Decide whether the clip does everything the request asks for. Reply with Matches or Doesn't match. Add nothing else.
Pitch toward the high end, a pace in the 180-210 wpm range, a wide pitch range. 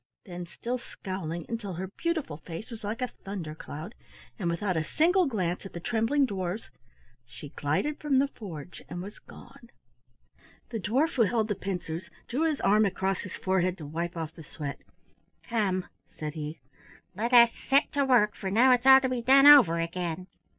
Matches